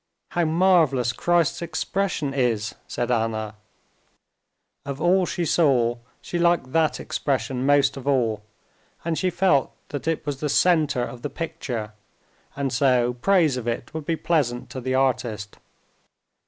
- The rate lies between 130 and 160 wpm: Yes, average, 145 wpm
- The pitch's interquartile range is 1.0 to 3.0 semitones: No, average, 5.1 semitones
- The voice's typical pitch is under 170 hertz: Yes, medium, 140 Hz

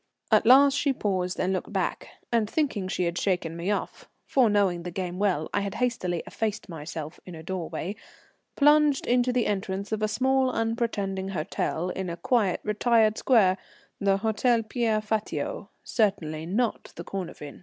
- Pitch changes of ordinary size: Yes, average, 4.3 semitones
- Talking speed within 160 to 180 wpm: Yes, average, 165 wpm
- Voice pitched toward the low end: No, high, 205 Hz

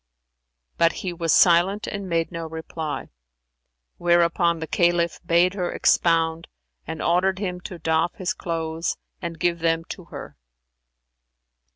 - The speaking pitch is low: No, medium, 170 Hz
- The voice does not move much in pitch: Yes, narrow, 1.3 semitones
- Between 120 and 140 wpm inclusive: Yes, slow, 135 wpm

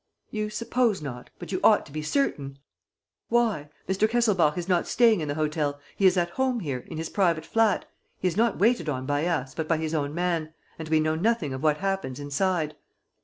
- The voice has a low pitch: No, medium, 165 Hz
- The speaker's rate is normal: No, fast, 215 wpm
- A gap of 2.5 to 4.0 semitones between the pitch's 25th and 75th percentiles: No, wide, 5.4 semitones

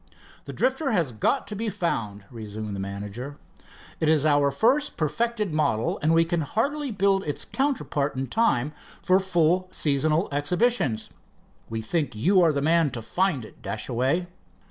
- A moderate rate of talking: Yes, average, 160 wpm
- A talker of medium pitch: Yes, medium, 155 Hz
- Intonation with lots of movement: Yes, wide, 7.1 semitones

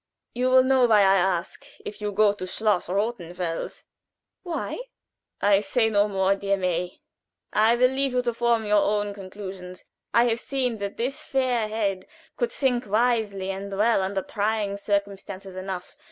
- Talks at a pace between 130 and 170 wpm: Yes, average, 165 wpm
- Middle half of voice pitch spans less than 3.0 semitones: No, average, 3.4 semitones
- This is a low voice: No, high, 205 Hz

